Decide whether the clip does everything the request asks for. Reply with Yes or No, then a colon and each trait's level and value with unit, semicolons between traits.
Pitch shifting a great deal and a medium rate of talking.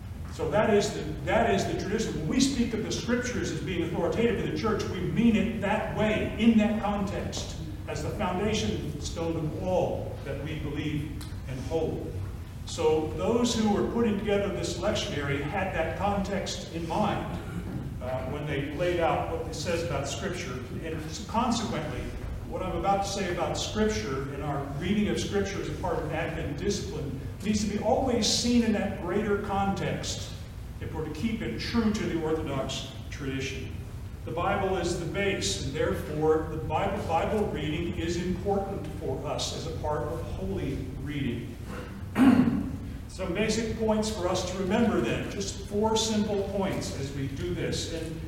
Yes: wide, 8.4 semitones; average, 170 wpm